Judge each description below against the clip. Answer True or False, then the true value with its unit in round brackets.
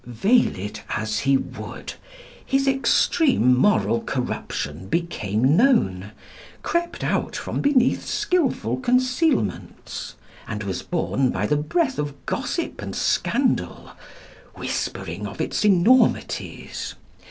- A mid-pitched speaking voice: True (150 Hz)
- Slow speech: True (110 wpm)